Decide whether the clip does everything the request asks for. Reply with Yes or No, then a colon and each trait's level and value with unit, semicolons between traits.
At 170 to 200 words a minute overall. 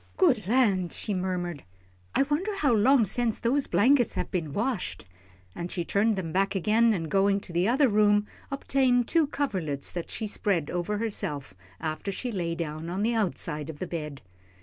Yes: average, 180 wpm